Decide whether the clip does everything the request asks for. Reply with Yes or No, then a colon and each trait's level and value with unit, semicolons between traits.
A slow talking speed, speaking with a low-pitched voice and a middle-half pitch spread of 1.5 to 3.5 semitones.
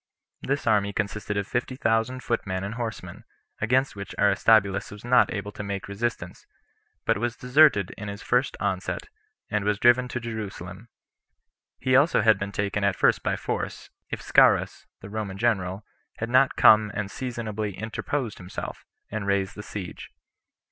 No: average, 160 wpm; low, 105 Hz; average, 3.1 semitones